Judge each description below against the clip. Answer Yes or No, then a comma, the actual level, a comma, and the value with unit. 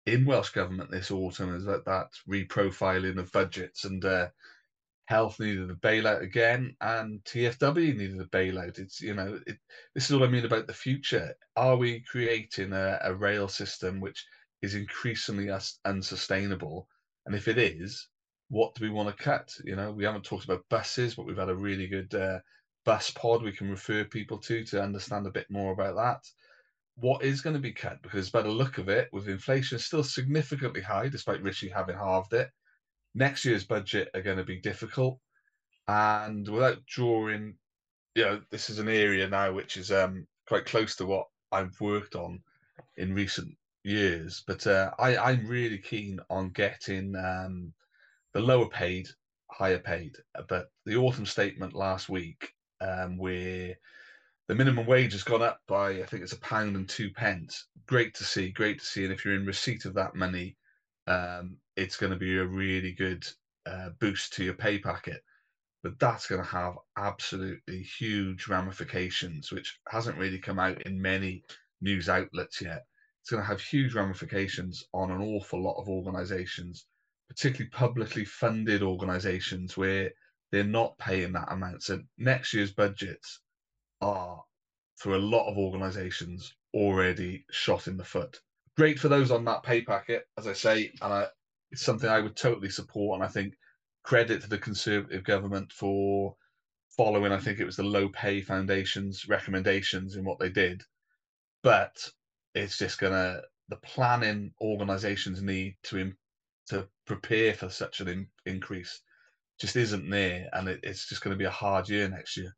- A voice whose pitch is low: Yes, low, 100 Hz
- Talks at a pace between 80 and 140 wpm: No, average, 175 wpm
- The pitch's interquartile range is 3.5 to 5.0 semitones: No, average, 2.9 semitones